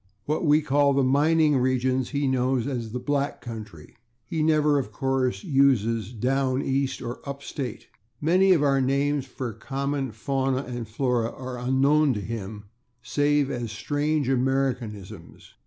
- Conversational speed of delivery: Yes, average, 155 wpm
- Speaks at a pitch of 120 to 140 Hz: Yes, low, 135 Hz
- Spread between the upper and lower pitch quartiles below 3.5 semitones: Yes, average, 2.7 semitones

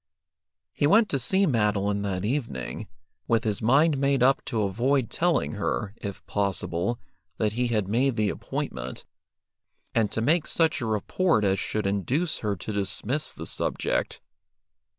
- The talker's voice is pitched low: Yes, low, 110 Hz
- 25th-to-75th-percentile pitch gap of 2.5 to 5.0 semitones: No, wide, 5.4 semitones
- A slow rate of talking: No, average, 150 wpm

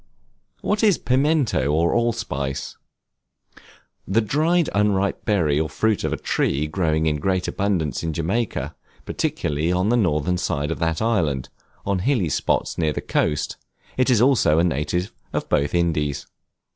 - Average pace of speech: Yes, average, 150 wpm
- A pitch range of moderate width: No, wide, 6.5 semitones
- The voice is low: Yes, very low, 90 Hz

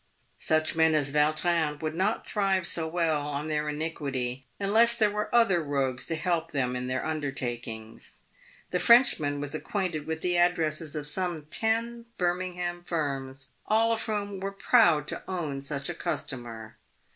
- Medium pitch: Yes, medium, 160 Hz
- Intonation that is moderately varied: Yes, average, 4.5 semitones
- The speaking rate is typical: Yes, average, 160 wpm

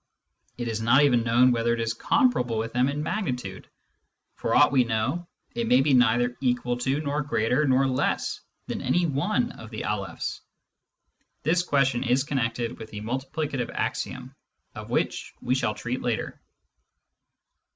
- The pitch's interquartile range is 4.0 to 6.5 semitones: No, average, 3.3 semitones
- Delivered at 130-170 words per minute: Yes, average, 160 wpm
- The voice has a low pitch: Yes, low, 125 Hz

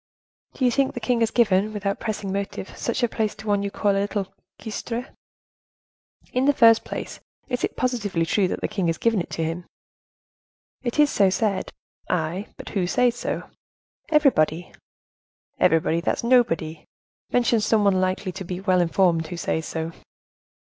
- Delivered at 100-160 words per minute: No, average, 175 wpm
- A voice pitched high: Yes, high, 200 Hz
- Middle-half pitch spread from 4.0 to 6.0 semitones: Yes, average, 4.5 semitones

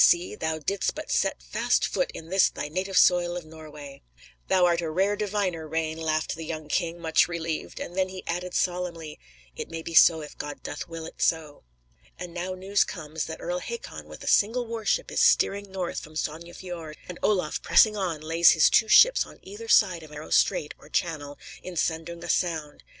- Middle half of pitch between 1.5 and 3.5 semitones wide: Yes, average, 2.8 semitones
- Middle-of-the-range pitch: Yes, medium, 170 Hz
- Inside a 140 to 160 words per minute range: No, fast, 205 wpm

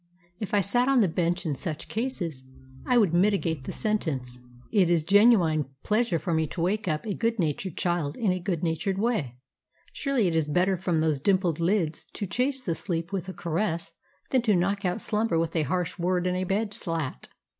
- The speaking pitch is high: No, medium, 180 Hz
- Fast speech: Yes, fast, 210 wpm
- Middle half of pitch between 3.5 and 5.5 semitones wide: Yes, average, 4.2 semitones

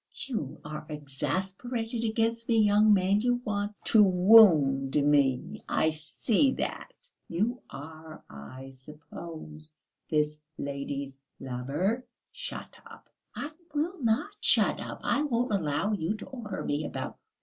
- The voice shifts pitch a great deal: Yes, wide, 7.4 semitones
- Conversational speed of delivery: No, slow, 125 wpm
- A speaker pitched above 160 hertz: Yes, medium, 185 Hz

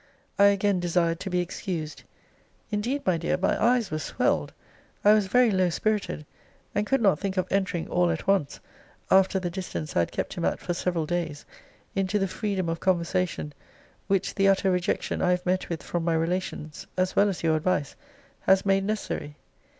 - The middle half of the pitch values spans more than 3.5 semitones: No, narrow, 2.6 semitones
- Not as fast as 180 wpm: No, average, 190 wpm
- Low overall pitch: No, medium, 185 Hz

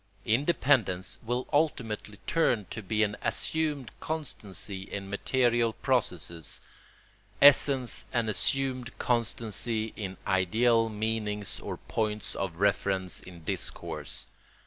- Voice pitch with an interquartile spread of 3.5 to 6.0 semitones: Yes, average, 4.2 semitones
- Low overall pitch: Yes, low, 110 Hz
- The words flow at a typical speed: No, slow, 105 wpm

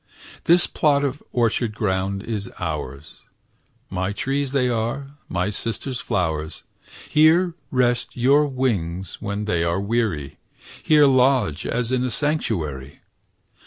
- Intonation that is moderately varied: No, wide, 6.7 semitones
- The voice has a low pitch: Yes, low, 115 Hz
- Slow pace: Yes, slow, 125 wpm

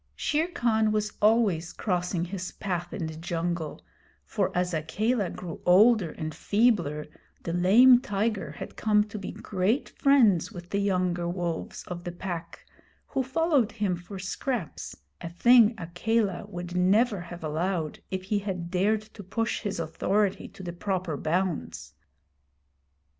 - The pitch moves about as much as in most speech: Yes, average, 3.7 semitones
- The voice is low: No, high, 190 Hz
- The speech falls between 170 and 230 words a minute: No, average, 145 wpm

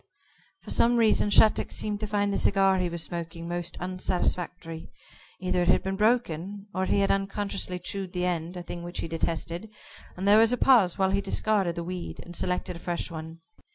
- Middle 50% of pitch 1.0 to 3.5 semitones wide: Yes, average, 2.7 semitones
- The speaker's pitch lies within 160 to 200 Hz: Yes, medium, 185 Hz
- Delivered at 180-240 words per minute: Yes, average, 200 wpm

